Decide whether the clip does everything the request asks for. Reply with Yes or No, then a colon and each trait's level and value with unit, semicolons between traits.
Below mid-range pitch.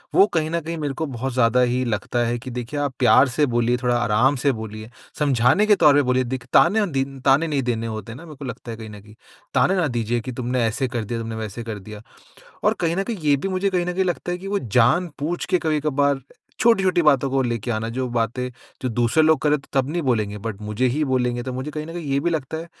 Yes: low, 130 Hz